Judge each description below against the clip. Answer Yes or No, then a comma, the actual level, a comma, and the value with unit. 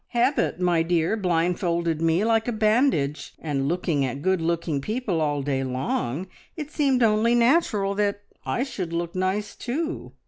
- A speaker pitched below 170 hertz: No, medium, 180 Hz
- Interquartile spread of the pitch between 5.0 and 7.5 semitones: Yes, wide, 5.6 semitones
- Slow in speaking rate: No, average, 160 wpm